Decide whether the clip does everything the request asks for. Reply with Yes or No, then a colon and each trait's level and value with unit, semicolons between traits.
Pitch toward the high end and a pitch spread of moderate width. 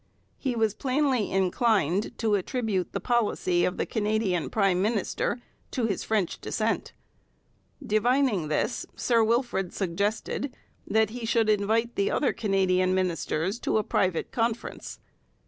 Yes: high, 215 Hz; average, 3.9 semitones